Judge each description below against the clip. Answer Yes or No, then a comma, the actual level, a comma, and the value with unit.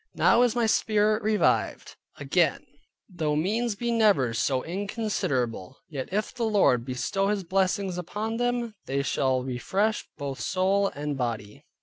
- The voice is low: No, high, 195 Hz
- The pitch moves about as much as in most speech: No, wide, 8.0 semitones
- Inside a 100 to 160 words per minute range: Yes, average, 140 wpm